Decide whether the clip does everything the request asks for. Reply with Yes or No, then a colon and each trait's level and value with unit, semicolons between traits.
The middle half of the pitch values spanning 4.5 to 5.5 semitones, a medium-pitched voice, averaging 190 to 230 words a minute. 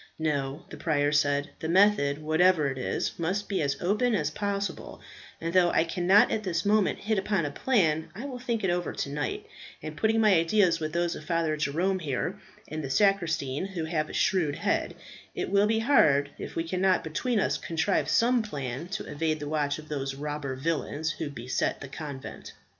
Yes: average, 5.0 semitones; medium, 165 Hz; average, 195 wpm